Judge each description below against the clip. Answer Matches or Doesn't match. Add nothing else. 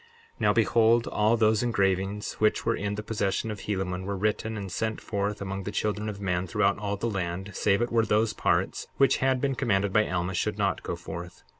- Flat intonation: Matches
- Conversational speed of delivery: Doesn't match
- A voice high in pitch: Doesn't match